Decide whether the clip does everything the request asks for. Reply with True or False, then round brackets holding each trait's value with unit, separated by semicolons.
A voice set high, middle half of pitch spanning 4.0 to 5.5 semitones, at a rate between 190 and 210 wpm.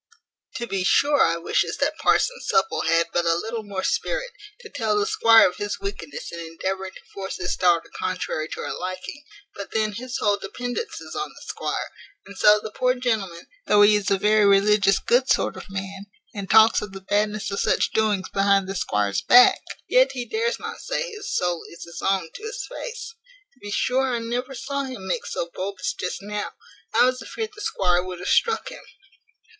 True (205 Hz; 4.8 semitones; 205 wpm)